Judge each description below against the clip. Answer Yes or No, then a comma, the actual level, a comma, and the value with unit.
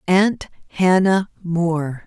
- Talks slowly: Yes, slow, 85 wpm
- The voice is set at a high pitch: No, medium, 175 Hz